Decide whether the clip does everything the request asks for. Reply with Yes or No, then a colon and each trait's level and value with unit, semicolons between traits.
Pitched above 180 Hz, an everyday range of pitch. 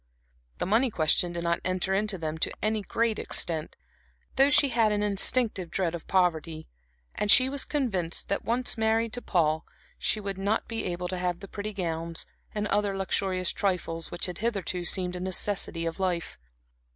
Yes: high, 190 Hz; average, 3.6 semitones